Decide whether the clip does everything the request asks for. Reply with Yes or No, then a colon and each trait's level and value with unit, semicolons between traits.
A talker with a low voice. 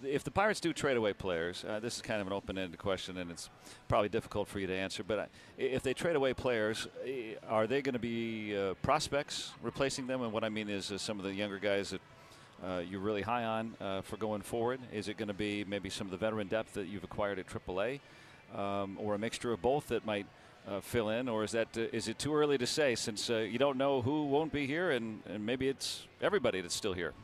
Yes: low, 110 Hz